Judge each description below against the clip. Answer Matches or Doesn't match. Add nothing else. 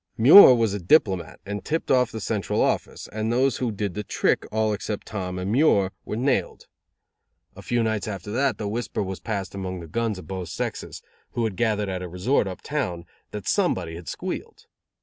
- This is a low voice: Matches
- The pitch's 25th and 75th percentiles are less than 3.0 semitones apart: Doesn't match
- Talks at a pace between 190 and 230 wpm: Matches